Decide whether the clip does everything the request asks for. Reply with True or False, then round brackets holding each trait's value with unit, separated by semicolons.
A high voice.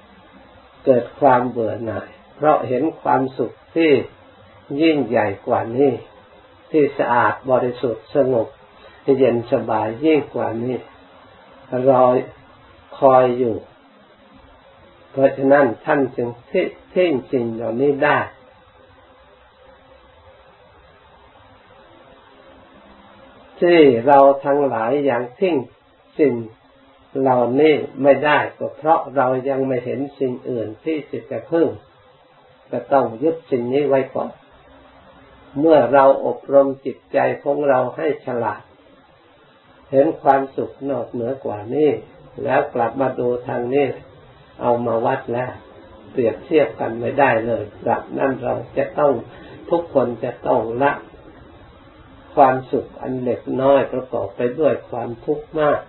False (130 Hz)